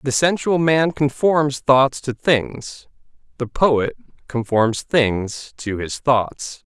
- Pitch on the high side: No, low, 135 Hz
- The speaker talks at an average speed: No, slow, 125 wpm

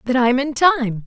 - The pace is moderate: No, fast, 225 wpm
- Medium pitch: No, very high, 260 Hz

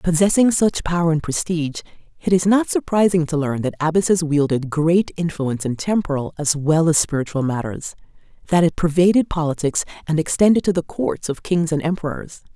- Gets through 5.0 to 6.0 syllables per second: Yes, 5.5 syllables/s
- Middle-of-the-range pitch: Yes, medium, 160 Hz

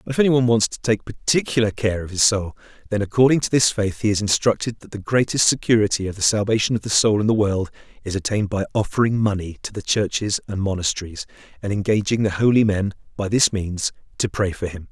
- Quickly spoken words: Yes, fast, 215 wpm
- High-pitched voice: No, low, 105 Hz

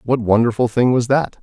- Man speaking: Yes, male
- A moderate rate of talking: No, fast, 210 wpm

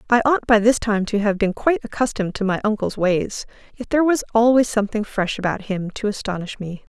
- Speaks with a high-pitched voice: Yes, high, 215 Hz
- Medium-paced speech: No, fast, 215 wpm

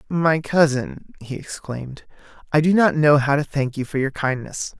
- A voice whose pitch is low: No, medium, 145 Hz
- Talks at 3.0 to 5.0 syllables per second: Yes, 4.7 syllables/s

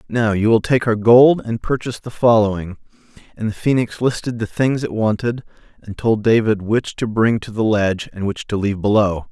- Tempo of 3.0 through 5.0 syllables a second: No, 5.3 syllables/s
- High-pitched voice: No, low, 110 Hz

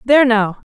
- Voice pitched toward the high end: Yes, high, 240 Hz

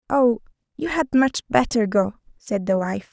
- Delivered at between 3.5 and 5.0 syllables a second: Yes, 4.8 syllables/s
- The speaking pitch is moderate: No, high, 235 Hz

